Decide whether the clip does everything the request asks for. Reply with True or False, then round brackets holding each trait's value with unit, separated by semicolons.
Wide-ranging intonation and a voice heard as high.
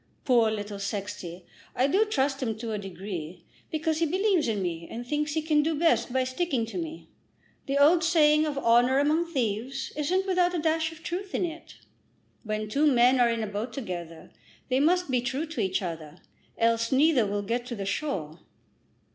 True (6.8 semitones; 260 Hz)